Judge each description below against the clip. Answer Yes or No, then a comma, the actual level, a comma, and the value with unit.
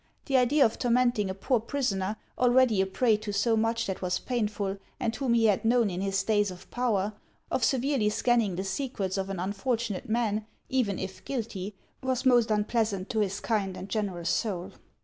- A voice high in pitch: Yes, high, 215 Hz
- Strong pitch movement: No, average, 3.8 semitones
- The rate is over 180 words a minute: Yes, average, 190 wpm